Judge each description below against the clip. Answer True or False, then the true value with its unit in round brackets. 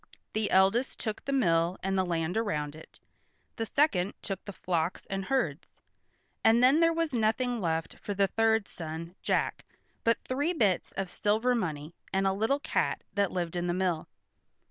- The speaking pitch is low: False (195 Hz)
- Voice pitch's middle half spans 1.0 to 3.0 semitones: False (4.8 semitones)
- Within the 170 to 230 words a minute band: True (175 wpm)